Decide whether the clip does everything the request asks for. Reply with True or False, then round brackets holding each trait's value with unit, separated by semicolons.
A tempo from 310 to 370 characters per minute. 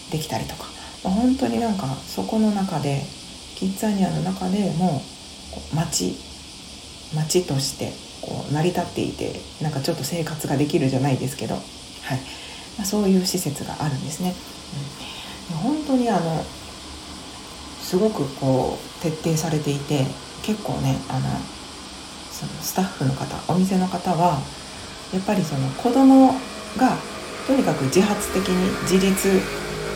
False (280 characters per minute)